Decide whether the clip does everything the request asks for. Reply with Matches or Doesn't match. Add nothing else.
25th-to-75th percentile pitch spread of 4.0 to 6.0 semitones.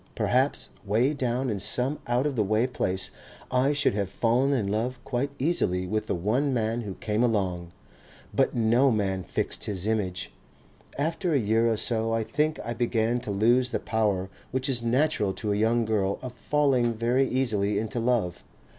Doesn't match